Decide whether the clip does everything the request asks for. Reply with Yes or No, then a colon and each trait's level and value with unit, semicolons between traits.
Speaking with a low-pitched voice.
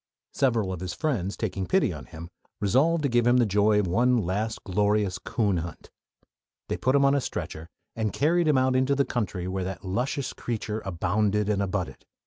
Yes: low, 105 Hz